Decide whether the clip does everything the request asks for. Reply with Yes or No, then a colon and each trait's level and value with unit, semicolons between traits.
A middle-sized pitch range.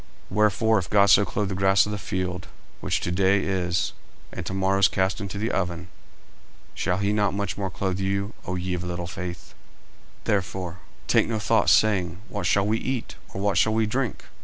No: narrow, 2.2 semitones